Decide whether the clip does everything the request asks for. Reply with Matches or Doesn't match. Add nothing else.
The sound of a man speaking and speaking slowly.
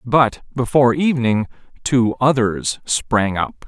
Matches